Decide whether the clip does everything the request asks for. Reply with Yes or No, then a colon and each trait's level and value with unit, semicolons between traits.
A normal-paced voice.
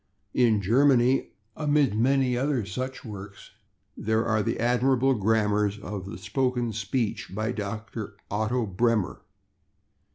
No: slow, 120 wpm